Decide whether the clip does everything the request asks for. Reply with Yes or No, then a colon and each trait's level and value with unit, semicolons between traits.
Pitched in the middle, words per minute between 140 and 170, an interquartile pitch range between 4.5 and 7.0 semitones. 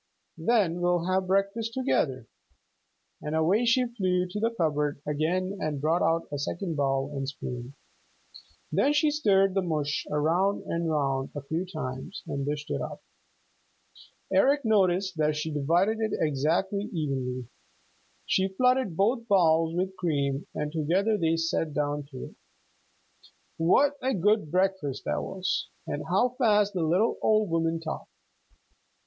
Yes: medium, 170 Hz; average, 145 wpm; average, 5.1 semitones